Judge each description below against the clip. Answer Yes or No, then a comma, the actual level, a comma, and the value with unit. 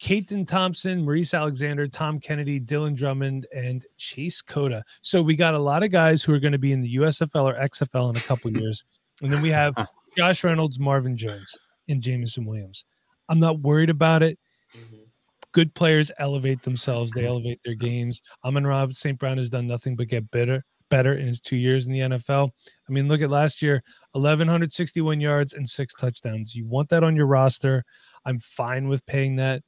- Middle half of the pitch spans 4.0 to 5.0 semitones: No, average, 3.3 semitones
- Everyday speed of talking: Yes, average, 195 wpm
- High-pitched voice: No, medium, 140 Hz